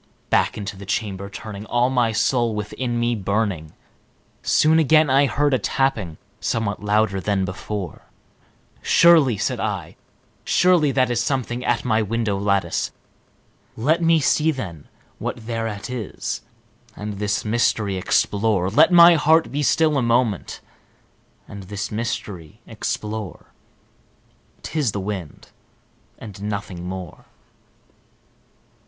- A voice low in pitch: Yes, low, 110 Hz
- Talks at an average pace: No, slow, 125 wpm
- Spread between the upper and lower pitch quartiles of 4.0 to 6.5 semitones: Yes, average, 4.6 semitones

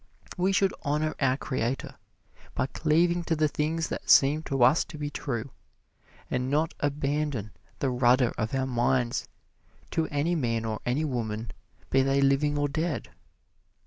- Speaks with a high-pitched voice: No, medium, 140 Hz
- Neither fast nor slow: Yes, average, 155 wpm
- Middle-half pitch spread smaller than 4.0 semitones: Yes, average, 3.4 semitones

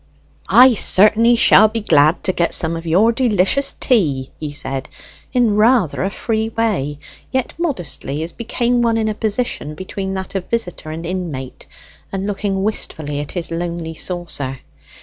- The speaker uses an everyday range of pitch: No, wide, 5.8 semitones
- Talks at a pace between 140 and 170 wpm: Yes, average, 160 wpm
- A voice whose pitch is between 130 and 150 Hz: No, high, 190 Hz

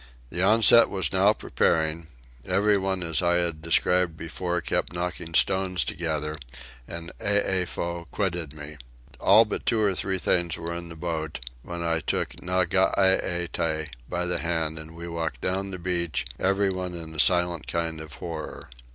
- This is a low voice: Yes, very low, 85 Hz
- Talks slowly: No, average, 155 wpm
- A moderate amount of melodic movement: No, narrow, 2.2 semitones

